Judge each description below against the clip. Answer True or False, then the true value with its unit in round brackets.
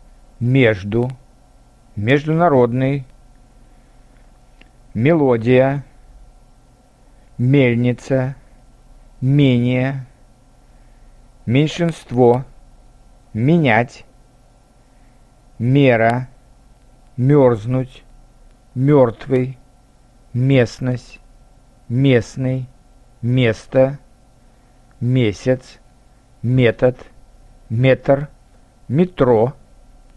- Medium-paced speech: False (35 wpm)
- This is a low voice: True (125 Hz)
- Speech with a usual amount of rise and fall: False (0.8 semitones)